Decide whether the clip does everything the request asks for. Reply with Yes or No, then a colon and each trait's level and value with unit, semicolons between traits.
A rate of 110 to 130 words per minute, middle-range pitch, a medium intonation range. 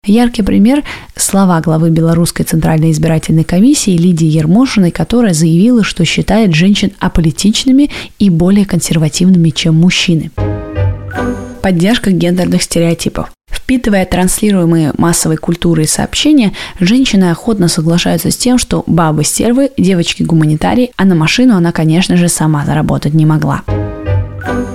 Yes: average, 120 wpm; medium, 175 Hz; average, 4.0 semitones